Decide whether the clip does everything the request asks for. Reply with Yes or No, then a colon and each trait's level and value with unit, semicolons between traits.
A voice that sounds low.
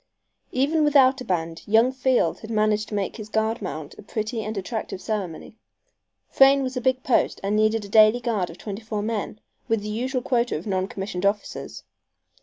No: high, 220 Hz